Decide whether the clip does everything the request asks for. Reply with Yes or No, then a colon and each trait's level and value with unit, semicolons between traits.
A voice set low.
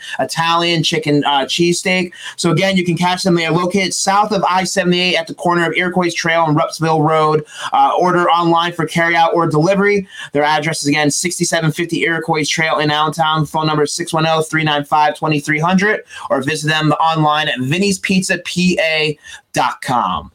No: medium, 165 Hz